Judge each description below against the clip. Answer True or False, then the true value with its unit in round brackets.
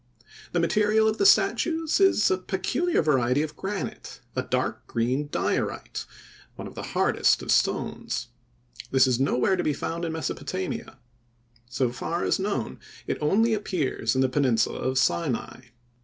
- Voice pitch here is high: False (155 Hz)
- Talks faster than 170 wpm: False (155 wpm)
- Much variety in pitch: True (7.6 semitones)